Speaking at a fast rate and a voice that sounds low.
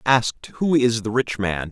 Yes: fast, 210 wpm; low, 115 Hz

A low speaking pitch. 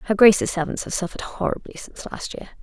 No: high, 195 Hz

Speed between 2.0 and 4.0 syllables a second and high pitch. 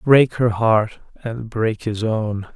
No: 3.1 syllables/s; low, 110 Hz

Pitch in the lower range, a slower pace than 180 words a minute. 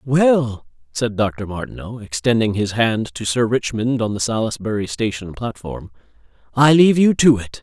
Yes: low, 115 Hz; average, 155 wpm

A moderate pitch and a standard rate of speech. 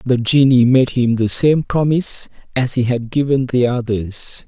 No: low, 125 Hz; average, 175 wpm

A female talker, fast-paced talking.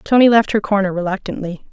No: female; average, 175 wpm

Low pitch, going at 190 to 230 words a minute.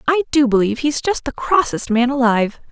No: very high, 260 Hz; average, 200 wpm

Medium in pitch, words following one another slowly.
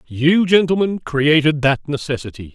Yes: medium, 150 Hz; slow, 120 wpm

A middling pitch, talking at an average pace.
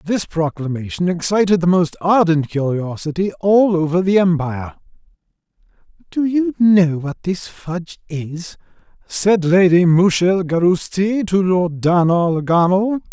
No: medium, 175 Hz; slow, 110 wpm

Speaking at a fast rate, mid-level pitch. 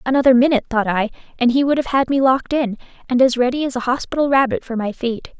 No: fast, 245 wpm; very high, 255 Hz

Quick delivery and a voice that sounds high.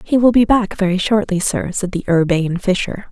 Yes: fast, 210 wpm; high, 200 Hz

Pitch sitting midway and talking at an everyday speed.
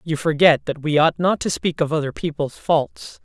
No: medium, 160 Hz; fast, 220 wpm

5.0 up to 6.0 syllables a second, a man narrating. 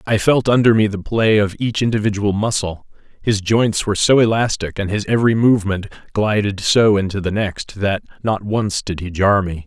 Yes: 5.1 syllables/s; male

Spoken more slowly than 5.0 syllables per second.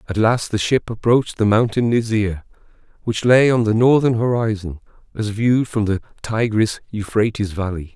No: 5.1 syllables/s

